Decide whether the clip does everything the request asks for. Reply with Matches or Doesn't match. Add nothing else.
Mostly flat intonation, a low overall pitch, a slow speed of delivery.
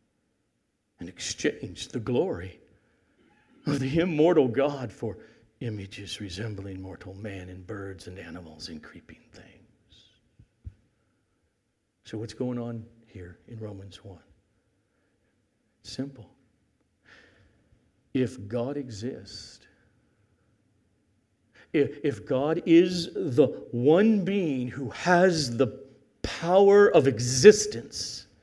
Doesn't match